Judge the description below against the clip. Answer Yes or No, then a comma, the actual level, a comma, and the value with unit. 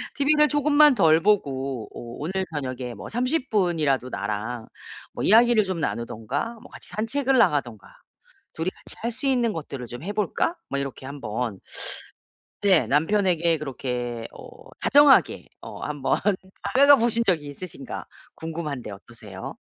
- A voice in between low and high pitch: Yes, medium, 160 Hz